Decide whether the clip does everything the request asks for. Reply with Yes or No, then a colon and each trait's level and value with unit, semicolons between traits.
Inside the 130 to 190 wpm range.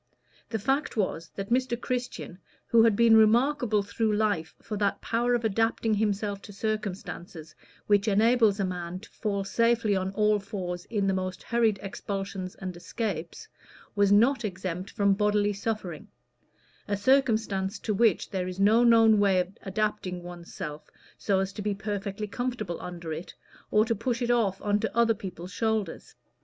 Yes: average, 170 wpm